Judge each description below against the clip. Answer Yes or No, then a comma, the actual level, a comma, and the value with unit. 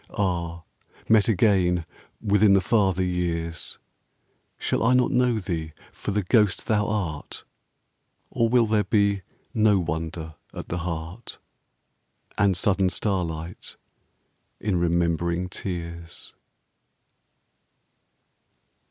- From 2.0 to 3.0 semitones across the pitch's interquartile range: No, average, 3.6 semitones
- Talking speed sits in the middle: No, slow, 100 wpm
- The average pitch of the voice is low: Yes, very low, 90 Hz